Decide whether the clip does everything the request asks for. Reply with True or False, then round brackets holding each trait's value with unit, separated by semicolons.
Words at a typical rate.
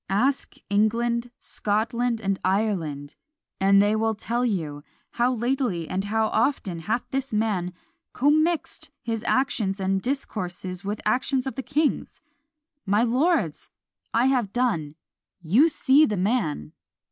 False (130 wpm)